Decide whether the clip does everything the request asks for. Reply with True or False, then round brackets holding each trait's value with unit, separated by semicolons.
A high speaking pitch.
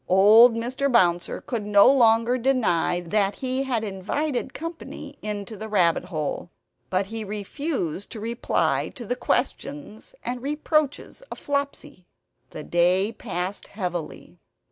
True (220 Hz)